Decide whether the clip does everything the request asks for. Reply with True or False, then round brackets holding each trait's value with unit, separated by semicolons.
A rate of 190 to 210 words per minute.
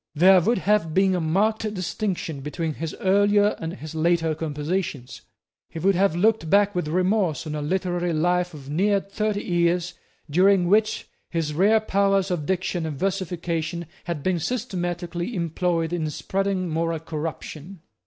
False (155 wpm)